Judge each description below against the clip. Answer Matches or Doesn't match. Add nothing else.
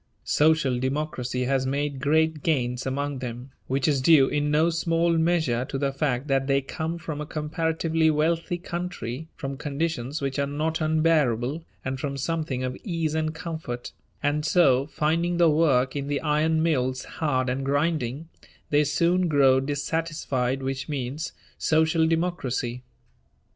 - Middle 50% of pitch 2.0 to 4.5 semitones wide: Matches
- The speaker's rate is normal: Matches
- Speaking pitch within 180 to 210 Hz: Doesn't match